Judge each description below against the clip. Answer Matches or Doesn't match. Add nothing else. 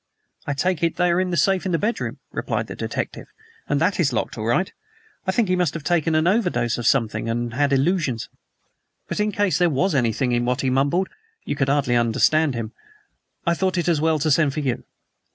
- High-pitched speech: Doesn't match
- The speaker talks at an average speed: Doesn't match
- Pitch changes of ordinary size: Doesn't match